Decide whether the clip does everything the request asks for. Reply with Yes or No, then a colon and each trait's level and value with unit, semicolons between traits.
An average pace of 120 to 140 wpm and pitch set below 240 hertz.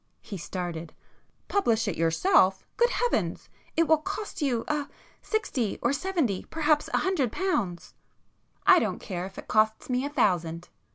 No: slow, 135 wpm; high, 245 Hz